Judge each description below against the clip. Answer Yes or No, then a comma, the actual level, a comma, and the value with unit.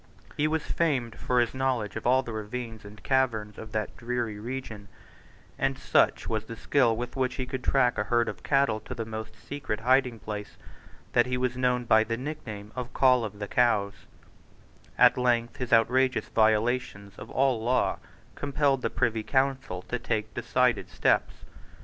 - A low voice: Yes, low, 120 Hz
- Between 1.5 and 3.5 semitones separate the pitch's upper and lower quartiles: Yes, average, 2.8 semitones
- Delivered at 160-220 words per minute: Yes, average, 175 wpm